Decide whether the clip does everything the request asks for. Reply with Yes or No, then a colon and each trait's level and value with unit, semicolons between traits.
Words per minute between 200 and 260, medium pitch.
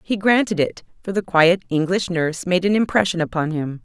Yes: fast, 205 wpm; medium, 175 Hz